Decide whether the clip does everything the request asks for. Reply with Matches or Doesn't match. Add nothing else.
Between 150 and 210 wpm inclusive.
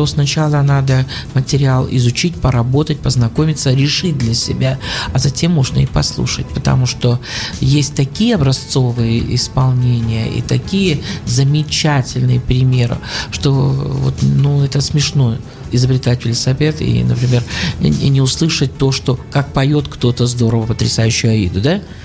Doesn't match